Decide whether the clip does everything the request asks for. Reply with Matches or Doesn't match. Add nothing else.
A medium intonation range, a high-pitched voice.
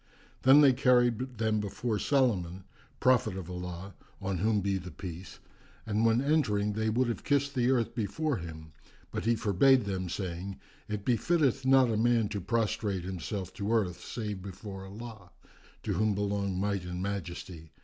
Doesn't match